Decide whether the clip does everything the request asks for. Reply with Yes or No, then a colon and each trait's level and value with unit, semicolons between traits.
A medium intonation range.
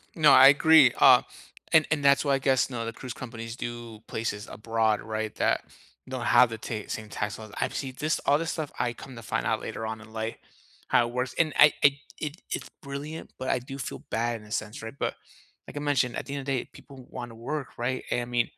Yes: average, 3.6 semitones